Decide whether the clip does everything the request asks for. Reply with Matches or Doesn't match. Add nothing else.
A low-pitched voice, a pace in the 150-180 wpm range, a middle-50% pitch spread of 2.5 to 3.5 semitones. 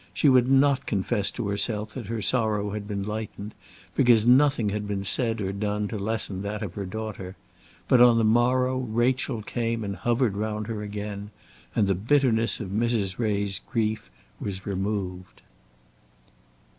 Matches